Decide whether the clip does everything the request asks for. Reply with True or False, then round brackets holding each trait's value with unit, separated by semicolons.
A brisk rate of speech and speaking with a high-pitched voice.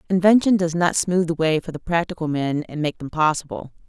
False (215 wpm; 165 Hz)